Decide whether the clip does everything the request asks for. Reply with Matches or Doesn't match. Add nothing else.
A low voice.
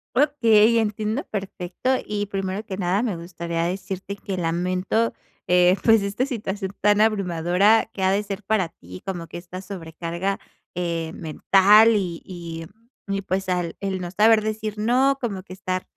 Doesn't match